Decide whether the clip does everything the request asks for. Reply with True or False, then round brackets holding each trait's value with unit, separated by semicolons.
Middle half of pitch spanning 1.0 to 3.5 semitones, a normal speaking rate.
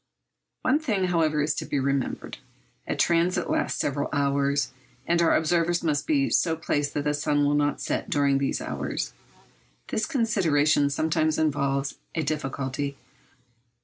True (2.9 semitones; 145 wpm)